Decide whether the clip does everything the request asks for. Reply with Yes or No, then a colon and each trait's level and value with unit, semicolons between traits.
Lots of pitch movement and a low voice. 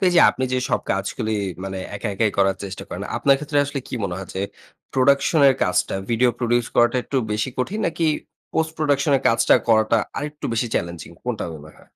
Yes: wide, 6.0 semitones; low, 120 Hz